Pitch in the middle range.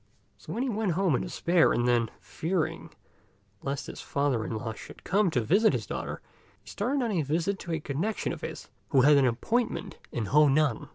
Yes: medium, 155 Hz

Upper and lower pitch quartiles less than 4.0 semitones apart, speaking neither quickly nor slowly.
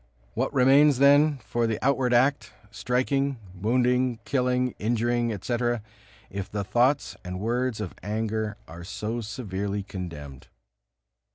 No: average, 3.6 semitones; slow, 120 wpm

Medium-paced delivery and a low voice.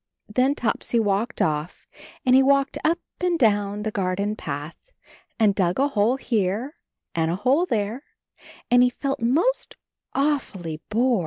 No: average, 155 wpm; high, 225 Hz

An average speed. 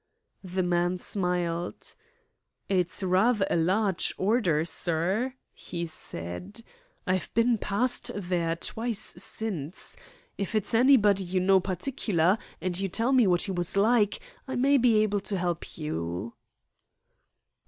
No: slow, 130 wpm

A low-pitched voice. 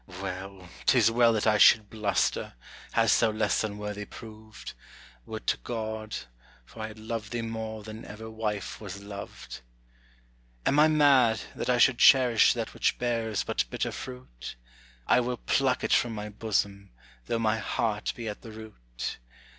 Yes: low, 110 Hz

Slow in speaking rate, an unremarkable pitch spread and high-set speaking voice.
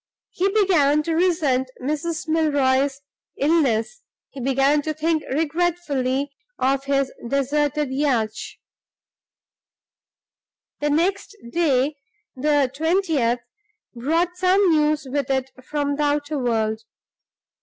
Yes: slow, 100 wpm; average, 3.3 semitones; very high, 290 Hz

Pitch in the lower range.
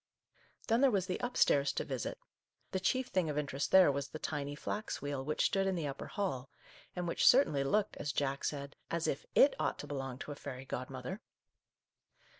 No: medium, 145 Hz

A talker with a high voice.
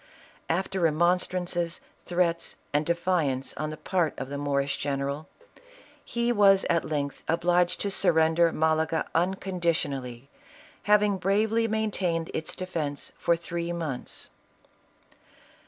No: medium, 170 Hz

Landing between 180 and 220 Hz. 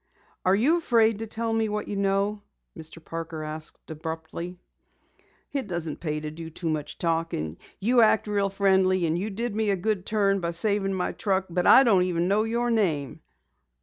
Yes: high, 190 Hz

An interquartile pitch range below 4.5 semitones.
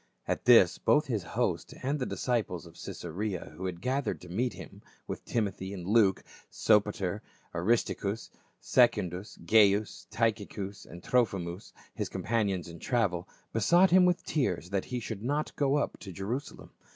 No: average, 4.8 semitones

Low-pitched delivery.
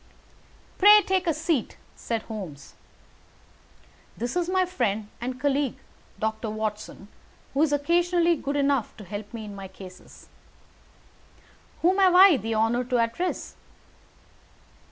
No: very high, 250 Hz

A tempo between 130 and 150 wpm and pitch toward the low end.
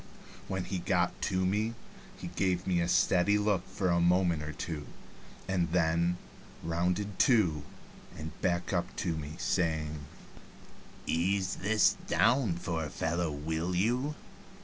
Yes: average, 140 wpm; very low, 90 Hz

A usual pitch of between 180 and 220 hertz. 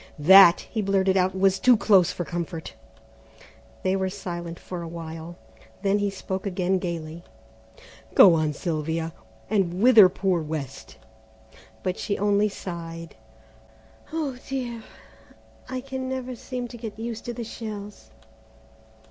Yes: high, 190 Hz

